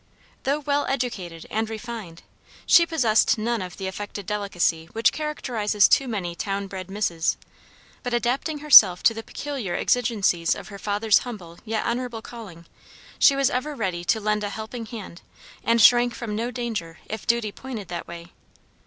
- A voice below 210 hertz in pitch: No, high, 220 Hz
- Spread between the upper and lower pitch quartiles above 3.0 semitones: Yes, average, 4.1 semitones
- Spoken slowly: No, average, 165 wpm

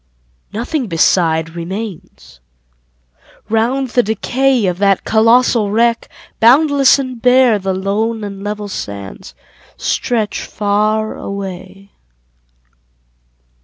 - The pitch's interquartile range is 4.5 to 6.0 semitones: No, average, 3.6 semitones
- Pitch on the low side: No, high, 215 Hz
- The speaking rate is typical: No, slow, 90 wpm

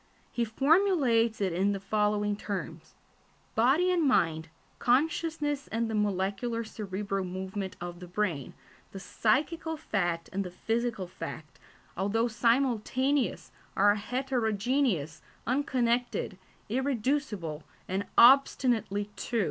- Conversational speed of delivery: No, slow, 110 wpm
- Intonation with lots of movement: No, average, 5.0 semitones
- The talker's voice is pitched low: No, high, 220 Hz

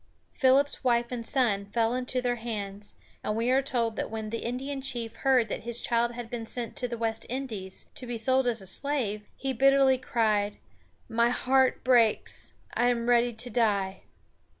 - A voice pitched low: No, high, 235 Hz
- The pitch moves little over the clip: Yes, narrow, 2.3 semitones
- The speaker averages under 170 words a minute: No, average, 185 wpm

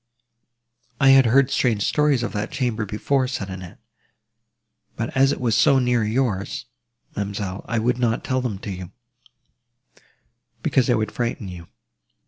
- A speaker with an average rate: Yes, average, 150 wpm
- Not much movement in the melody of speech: No, average, 4.0 semitones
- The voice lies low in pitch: Yes, low, 115 Hz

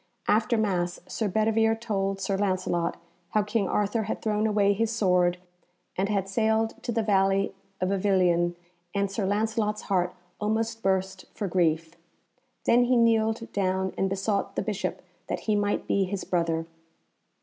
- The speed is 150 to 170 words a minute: Yes, average, 155 wpm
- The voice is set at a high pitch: Yes, high, 200 Hz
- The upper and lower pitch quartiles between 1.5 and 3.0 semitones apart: Yes, narrow, 2.6 semitones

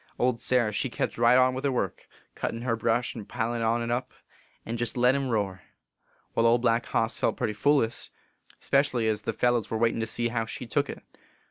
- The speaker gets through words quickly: Yes, fast, 220 wpm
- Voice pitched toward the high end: No, low, 120 Hz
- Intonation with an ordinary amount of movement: No, narrow, 1.7 semitones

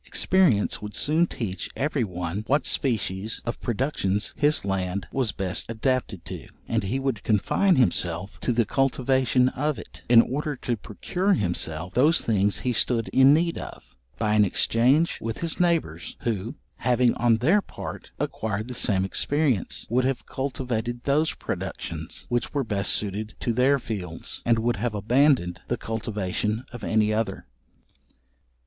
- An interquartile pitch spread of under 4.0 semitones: No, average, 4.6 semitones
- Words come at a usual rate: Yes, average, 155 wpm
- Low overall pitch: Yes, low, 115 Hz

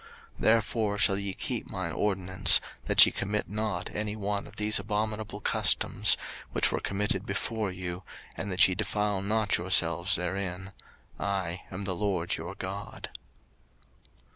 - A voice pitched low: Yes, low, 100 Hz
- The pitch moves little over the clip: Yes, narrow, 2.2 semitones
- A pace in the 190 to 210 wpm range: No, average, 145 wpm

